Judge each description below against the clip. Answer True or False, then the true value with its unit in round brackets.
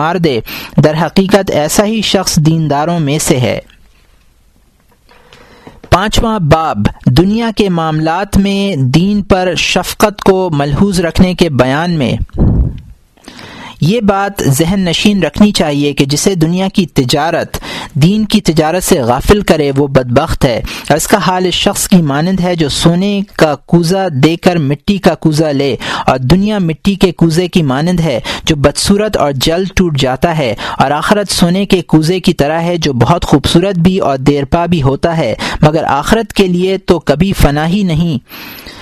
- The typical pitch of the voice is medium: True (175 Hz)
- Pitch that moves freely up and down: False (4.2 semitones)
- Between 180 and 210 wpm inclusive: False (160 wpm)